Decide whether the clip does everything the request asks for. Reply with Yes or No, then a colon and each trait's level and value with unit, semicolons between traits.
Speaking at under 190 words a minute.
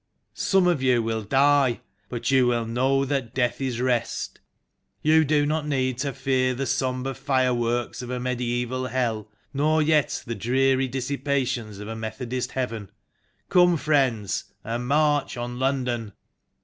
Yes: average, 150 wpm